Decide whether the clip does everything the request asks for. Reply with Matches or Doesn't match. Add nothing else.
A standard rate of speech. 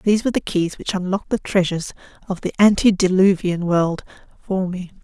Matches